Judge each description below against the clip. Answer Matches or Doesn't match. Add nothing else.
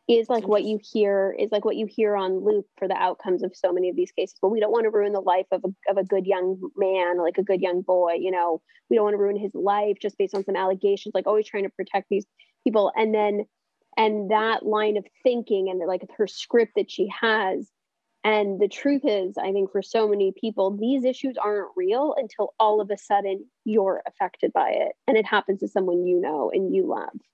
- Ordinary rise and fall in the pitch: Doesn't match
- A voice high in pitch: Matches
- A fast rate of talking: Matches